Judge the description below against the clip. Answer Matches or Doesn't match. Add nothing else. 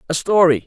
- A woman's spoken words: Doesn't match